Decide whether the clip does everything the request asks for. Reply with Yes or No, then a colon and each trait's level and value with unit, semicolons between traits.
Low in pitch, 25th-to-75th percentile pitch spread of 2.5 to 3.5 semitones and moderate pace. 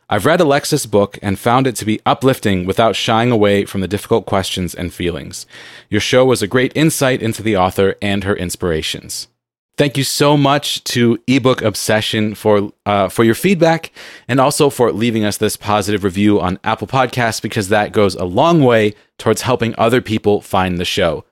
No: low, 110 Hz; average, 3.9 semitones; average, 190 wpm